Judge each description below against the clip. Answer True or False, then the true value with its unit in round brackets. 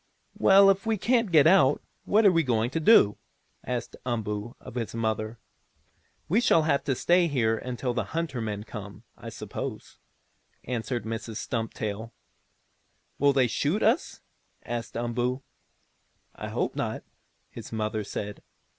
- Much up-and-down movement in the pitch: True (6.6 semitones)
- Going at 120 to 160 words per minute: True (145 wpm)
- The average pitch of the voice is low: True (125 Hz)